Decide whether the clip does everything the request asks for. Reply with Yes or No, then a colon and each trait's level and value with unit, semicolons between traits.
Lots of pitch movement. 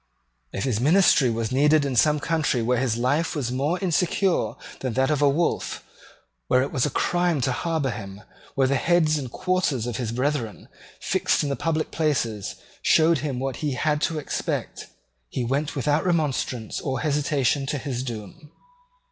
No: average, 3.7 semitones